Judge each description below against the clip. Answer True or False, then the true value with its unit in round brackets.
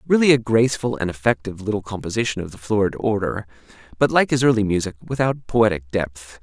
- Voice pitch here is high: False (105 Hz)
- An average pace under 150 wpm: False (175 wpm)